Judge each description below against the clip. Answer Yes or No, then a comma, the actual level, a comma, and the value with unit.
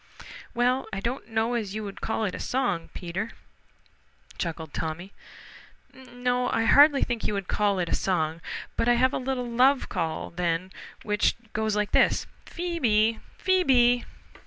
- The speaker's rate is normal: Yes, average, 165 wpm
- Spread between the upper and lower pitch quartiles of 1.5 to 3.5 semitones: No, average, 4.4 semitones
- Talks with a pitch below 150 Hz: No, high, 225 Hz